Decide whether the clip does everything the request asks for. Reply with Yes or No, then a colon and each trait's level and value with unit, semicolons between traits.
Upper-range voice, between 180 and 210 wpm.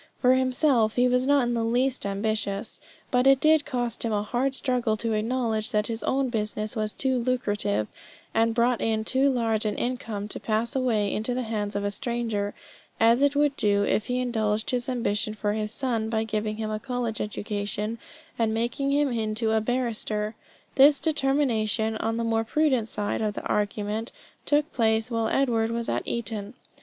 Yes: high, 225 Hz; average, 185 wpm